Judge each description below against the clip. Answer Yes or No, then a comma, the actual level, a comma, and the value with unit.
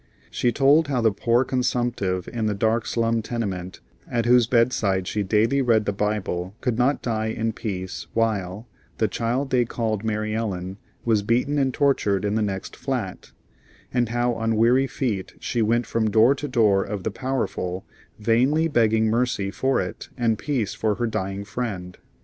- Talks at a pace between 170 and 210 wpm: Yes, average, 175 wpm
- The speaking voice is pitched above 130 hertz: No, low, 115 Hz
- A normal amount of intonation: Yes, average, 3.0 semitones